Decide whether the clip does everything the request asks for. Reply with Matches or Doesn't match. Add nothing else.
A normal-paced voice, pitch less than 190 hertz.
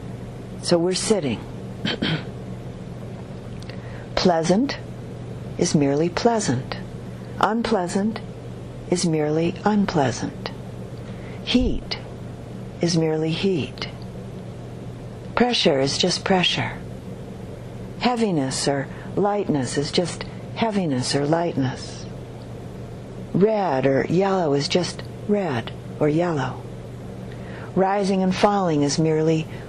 Doesn't match